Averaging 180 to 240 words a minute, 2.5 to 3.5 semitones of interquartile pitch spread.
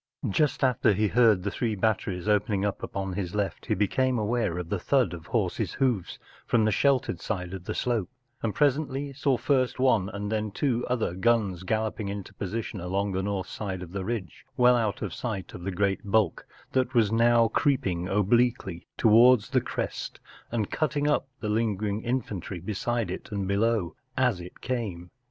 No: average, 185 wpm; average, 3.9 semitones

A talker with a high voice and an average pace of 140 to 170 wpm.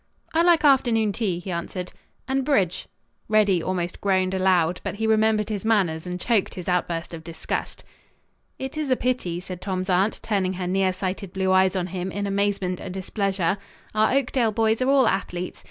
No: high, 195 Hz; average, 180 wpm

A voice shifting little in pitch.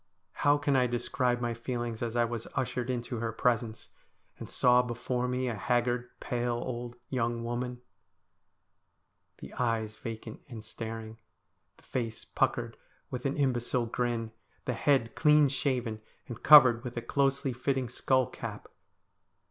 Yes: narrow, 1.6 semitones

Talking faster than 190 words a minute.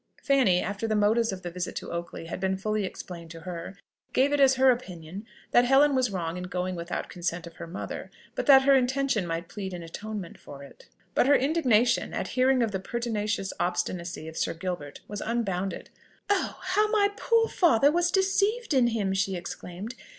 Yes: average, 200 wpm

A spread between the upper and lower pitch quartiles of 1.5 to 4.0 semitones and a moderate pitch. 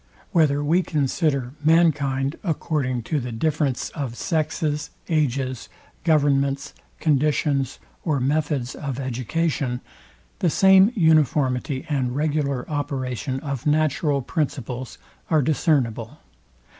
Yes: average, 3.0 semitones; medium, 145 Hz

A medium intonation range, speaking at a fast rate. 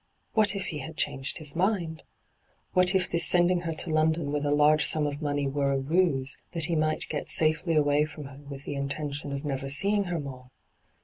Yes: average, 3.1 semitones; fast, 210 wpm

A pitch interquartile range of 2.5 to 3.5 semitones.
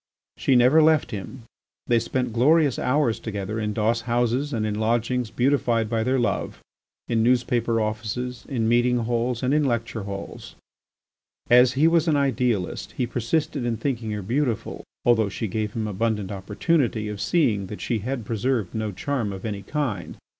Yes: average, 2.9 semitones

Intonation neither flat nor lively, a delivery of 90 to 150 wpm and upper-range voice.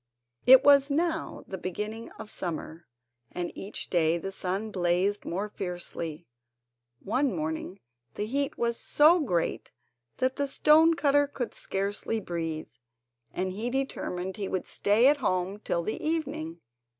No: wide, 7.2 semitones; average, 140 wpm; high, 205 Hz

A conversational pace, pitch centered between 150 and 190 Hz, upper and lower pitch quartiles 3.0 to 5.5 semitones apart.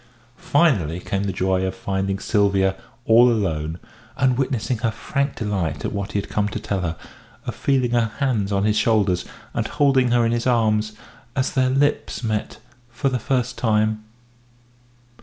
No: average, 170 wpm; low, 110 Hz; average, 4.3 semitones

